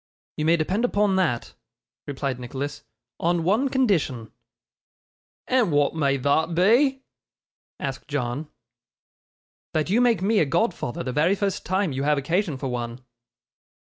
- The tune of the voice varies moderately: No, wide, 6.5 semitones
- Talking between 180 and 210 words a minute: No, slow, 135 wpm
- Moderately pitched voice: Yes, medium, 160 Hz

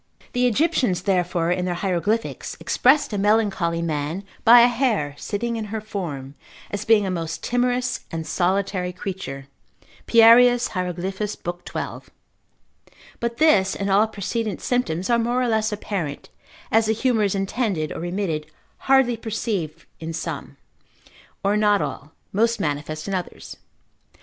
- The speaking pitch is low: No, high, 200 Hz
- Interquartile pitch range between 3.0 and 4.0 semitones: No, average, 4.7 semitones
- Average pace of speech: Yes, average, 145 wpm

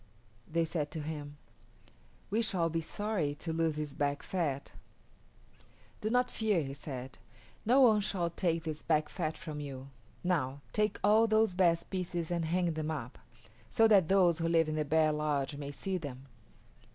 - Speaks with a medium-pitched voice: Yes, medium, 165 Hz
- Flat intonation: No, average, 3.9 semitones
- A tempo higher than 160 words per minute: Yes, average, 175 wpm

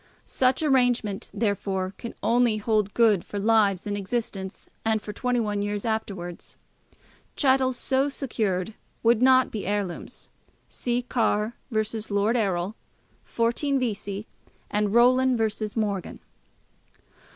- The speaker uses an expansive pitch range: No, average, 3.4 semitones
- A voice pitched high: Yes, high, 220 Hz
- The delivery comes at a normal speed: No, slow, 120 wpm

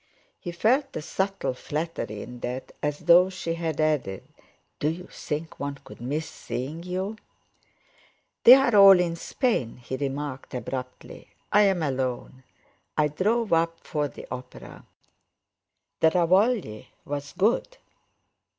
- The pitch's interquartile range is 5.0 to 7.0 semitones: Yes, wide, 5.6 semitones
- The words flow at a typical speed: No, slow, 125 wpm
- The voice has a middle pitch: Yes, medium, 160 Hz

